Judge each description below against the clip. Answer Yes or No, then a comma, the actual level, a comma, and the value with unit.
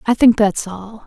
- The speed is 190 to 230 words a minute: Yes, fast, 225 wpm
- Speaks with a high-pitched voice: Yes, high, 215 Hz